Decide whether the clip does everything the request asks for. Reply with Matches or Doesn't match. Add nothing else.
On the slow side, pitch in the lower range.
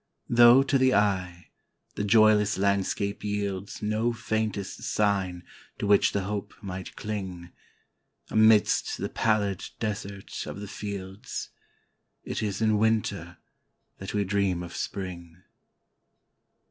Matches